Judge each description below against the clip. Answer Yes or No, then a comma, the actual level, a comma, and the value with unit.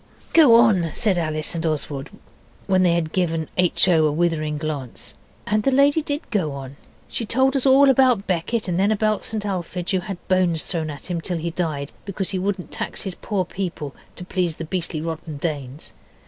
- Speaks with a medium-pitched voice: Yes, medium, 180 Hz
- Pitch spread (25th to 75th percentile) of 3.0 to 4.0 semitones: No, average, 4.5 semitones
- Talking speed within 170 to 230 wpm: Yes, average, 200 wpm